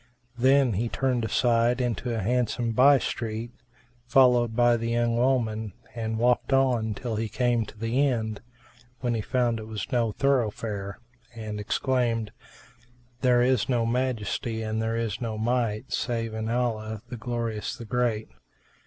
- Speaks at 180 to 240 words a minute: No, average, 155 wpm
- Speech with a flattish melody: Yes, narrow, 1.9 semitones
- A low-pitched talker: Yes, low, 115 Hz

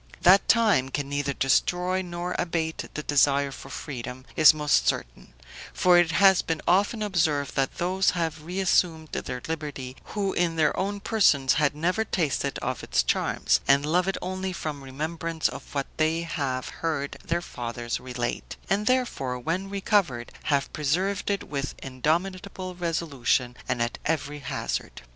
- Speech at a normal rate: Yes, average, 155 wpm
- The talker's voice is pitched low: No, medium, 160 Hz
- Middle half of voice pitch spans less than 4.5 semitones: No, average, 4.8 semitones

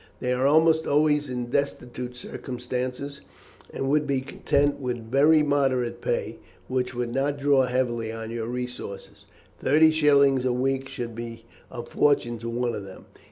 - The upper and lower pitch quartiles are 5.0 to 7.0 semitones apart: No, average, 2.7 semitones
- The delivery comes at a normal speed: Yes, average, 160 wpm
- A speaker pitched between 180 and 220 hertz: No, low, 130 Hz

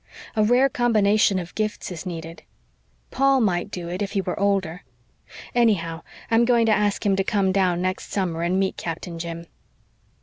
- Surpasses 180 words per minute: No, average, 175 wpm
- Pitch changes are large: No, average, 3.5 semitones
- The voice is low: No, high, 195 Hz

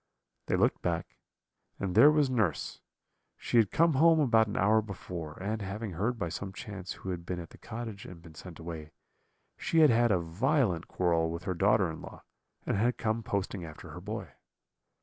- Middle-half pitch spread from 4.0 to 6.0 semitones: Yes, average, 5.0 semitones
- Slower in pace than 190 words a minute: No, average, 195 wpm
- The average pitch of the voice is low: Yes, low, 100 Hz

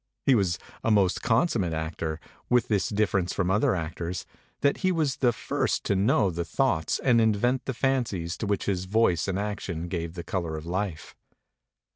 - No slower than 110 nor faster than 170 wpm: No, average, 185 wpm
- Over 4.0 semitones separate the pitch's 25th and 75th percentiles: Yes, average, 5.0 semitones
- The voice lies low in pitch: Yes, low, 100 Hz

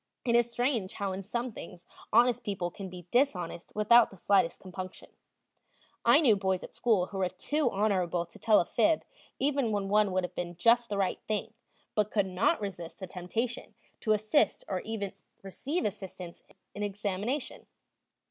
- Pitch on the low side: No, high, 205 Hz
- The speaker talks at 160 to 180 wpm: Yes, average, 175 wpm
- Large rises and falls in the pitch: No, average, 4.1 semitones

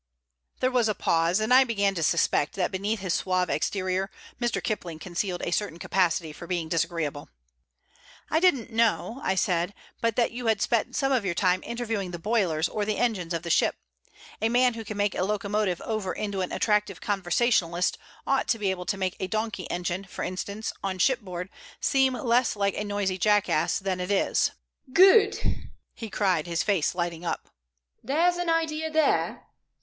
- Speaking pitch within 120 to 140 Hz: No, high, 200 Hz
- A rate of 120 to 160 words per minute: No, average, 185 wpm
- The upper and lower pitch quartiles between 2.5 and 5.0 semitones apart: Yes, average, 4.2 semitones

